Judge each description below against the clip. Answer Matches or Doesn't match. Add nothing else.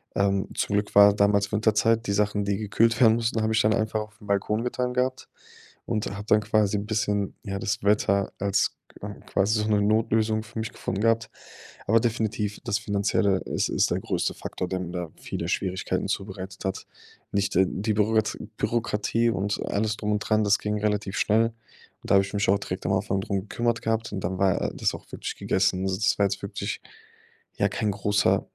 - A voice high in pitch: Doesn't match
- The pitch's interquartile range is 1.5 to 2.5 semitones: Matches